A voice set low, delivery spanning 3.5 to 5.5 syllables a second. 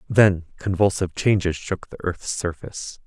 Yes: very low, 95 Hz; 4.9 syllables/s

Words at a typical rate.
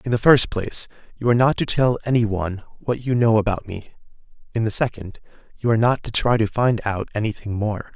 No: fast, 220 wpm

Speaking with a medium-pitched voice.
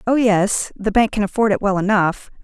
No: high, 205 Hz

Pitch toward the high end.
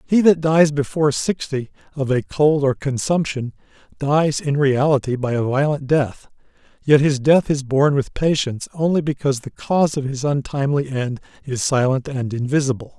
No: medium, 140 Hz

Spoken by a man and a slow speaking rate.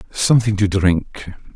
Yes: male; slow, 115 wpm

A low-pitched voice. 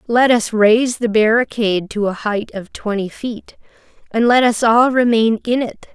No: high, 225 Hz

